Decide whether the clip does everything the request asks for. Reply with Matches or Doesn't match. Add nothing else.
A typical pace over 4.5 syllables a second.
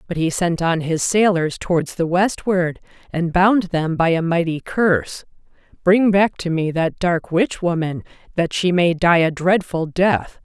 Doesn't match